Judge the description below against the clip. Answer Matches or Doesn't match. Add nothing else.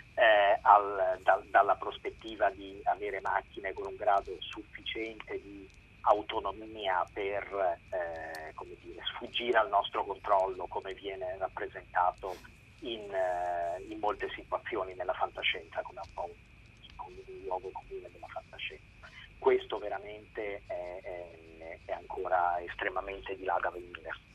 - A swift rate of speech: Doesn't match